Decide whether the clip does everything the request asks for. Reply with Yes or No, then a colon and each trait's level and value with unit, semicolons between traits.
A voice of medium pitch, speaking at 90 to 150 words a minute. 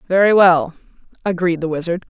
Yes: medium, 175 Hz; average, 140 wpm